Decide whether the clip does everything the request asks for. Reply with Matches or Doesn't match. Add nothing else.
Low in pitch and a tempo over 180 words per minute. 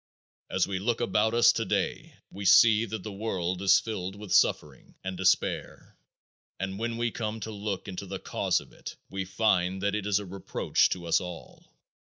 Matches